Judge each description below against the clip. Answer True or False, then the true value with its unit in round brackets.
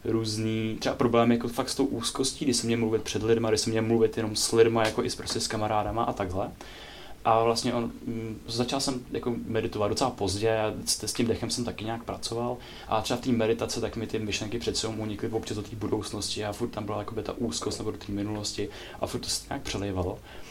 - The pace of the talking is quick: True (240 wpm)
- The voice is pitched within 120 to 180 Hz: False (110 Hz)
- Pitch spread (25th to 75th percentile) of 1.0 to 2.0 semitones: True (1.7 semitones)